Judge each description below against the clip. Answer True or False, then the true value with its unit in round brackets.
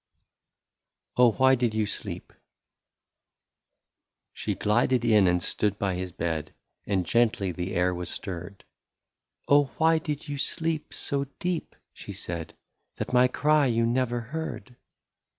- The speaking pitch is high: False (115 Hz)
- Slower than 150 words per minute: True (140 wpm)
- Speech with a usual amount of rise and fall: False (6.9 semitones)